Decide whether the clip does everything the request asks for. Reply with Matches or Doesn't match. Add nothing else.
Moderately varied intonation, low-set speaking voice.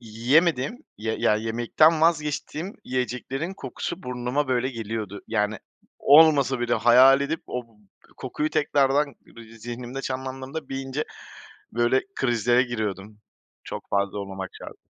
Matches